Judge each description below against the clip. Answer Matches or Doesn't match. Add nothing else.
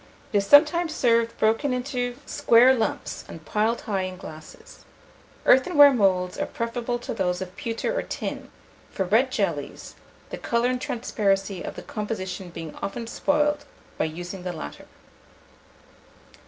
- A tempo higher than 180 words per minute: Doesn't match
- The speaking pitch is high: Matches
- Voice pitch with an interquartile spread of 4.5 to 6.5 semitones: Matches